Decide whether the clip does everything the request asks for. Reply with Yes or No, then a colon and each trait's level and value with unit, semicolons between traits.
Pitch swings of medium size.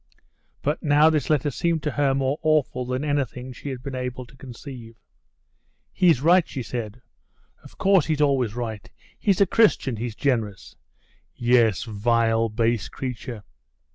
Yes: average, 4.0 semitones